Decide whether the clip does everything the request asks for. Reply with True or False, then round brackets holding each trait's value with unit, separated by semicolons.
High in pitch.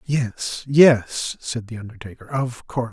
False (120 Hz)